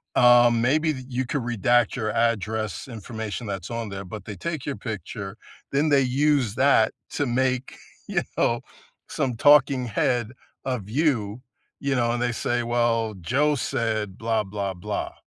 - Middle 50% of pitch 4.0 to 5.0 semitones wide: No, average, 3.3 semitones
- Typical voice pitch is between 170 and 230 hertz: No, low, 120 Hz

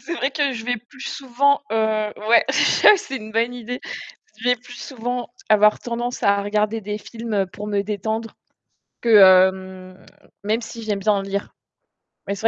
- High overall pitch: Yes, high, 220 Hz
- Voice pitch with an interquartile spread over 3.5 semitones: No, average, 3.2 semitones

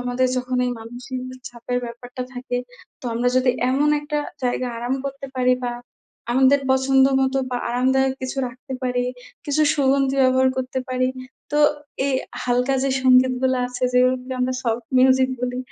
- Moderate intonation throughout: No, narrow, 1.1 semitones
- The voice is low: No, very high, 255 Hz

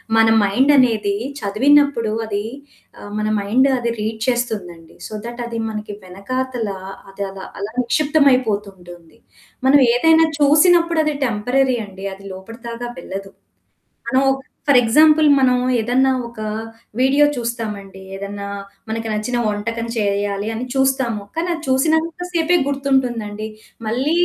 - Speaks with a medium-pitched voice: No, high, 235 Hz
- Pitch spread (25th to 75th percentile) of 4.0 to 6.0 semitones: Yes, average, 4.7 semitones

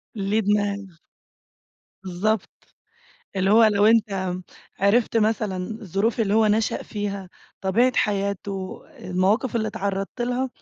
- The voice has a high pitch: Yes, high, 205 Hz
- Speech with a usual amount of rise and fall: No, narrow, 2.3 semitones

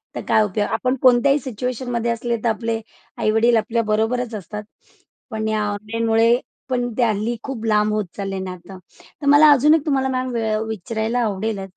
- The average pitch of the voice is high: Yes, high, 225 Hz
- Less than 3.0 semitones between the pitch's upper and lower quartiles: Yes, narrow, 2.5 semitones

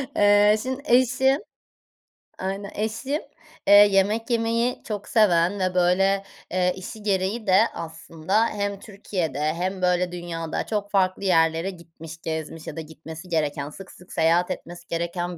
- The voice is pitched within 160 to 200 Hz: Yes, medium, 185 Hz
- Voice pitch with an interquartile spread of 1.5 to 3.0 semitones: No, average, 3.7 semitones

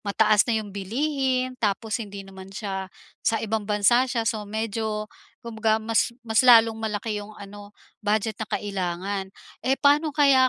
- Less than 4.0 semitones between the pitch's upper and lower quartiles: Yes, narrow, 2.4 semitones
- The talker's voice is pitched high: Yes, high, 220 Hz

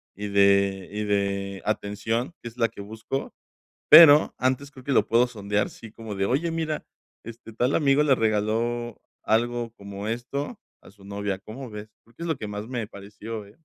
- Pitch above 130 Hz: No, low, 110 Hz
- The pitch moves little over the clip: No, average, 3.5 semitones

